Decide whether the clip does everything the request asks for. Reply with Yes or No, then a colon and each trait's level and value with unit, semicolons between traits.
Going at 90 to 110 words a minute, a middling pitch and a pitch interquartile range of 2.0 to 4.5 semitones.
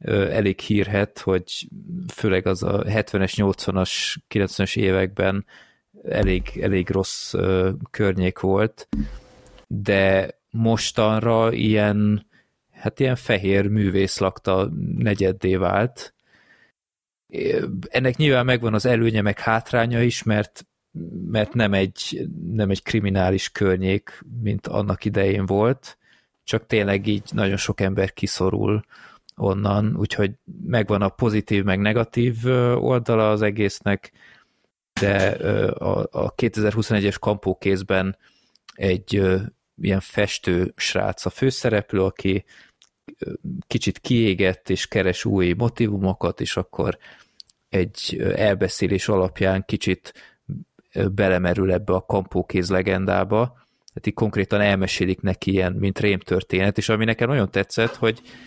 No: slow, 105 wpm; low, 100 Hz; average, 2.8 semitones